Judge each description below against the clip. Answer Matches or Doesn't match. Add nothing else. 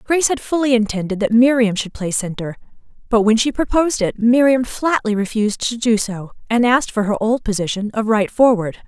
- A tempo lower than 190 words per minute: Doesn't match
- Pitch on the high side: Matches